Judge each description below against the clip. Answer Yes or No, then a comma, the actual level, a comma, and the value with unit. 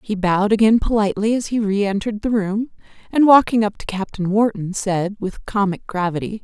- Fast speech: No, average, 175 wpm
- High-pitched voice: Yes, high, 205 Hz